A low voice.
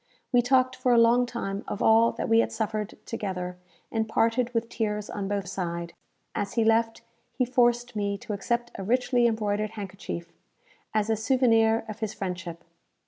No: high, 220 Hz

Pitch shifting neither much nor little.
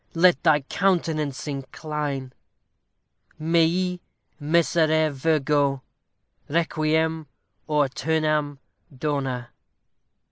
No: narrow, 2.2 semitones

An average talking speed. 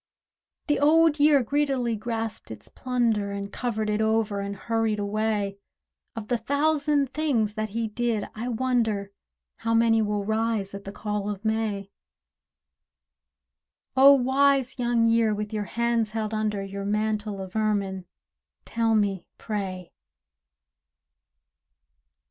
No: slow, 130 wpm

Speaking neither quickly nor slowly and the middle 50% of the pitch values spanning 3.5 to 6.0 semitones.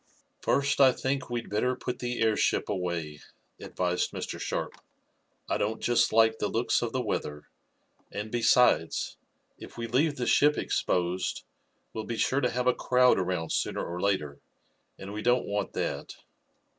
Yes: average, 160 wpm; average, 5.2 semitones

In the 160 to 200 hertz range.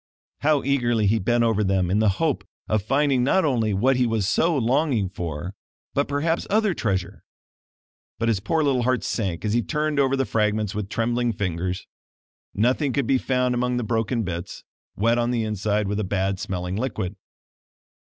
No: low, 115 Hz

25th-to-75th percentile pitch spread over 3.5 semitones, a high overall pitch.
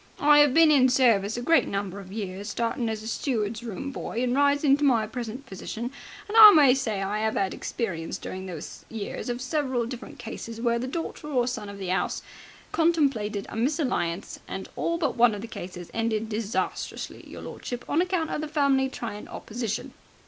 Yes: average, 4.9 semitones; high, 235 Hz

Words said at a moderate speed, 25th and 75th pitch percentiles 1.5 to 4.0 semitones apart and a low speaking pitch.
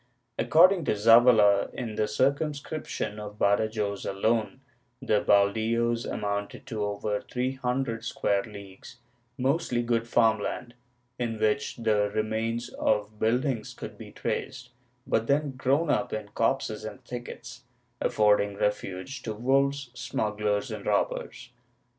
No: slow, 125 wpm; average, 3.4 semitones; low, 115 Hz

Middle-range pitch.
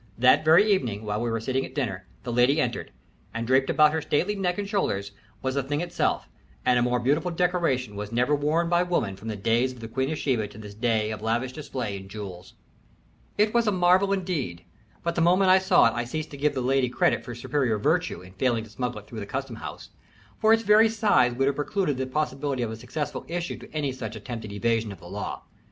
No: low, 130 Hz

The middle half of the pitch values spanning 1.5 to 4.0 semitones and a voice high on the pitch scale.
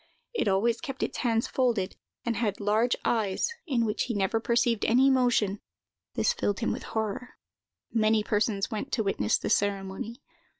Yes: average, 2.9 semitones; high, 225 Hz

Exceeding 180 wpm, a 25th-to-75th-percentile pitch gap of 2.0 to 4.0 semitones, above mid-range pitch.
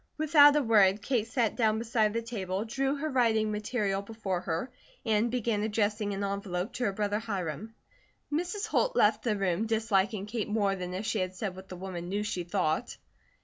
Yes: average, 190 wpm; average, 3.0 semitones; high, 210 Hz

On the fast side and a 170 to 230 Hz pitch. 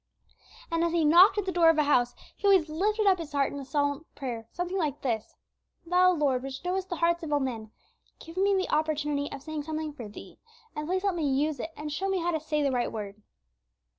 No: fast, 240 wpm; very high, 310 Hz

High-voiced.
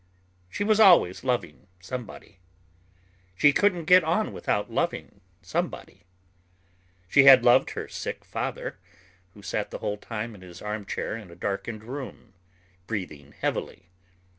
No: low, 110 Hz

